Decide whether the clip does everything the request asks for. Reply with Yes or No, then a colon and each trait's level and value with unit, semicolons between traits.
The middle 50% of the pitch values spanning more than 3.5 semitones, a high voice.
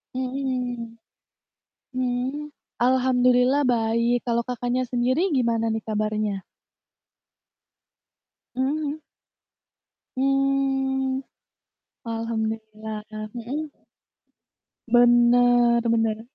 No: narrow, 2.4 semitones; high, 245 Hz